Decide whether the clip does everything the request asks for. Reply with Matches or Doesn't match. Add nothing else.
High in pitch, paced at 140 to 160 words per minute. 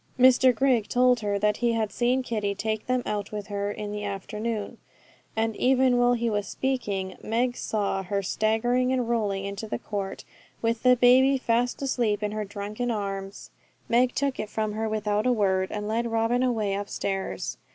Doesn't match